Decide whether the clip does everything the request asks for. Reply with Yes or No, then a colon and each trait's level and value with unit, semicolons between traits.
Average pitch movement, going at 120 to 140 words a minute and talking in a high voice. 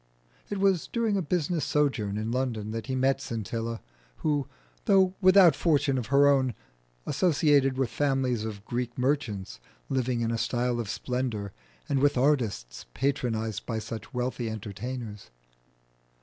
No: average, 4.1 semitones; slow, 135 wpm; low, 125 Hz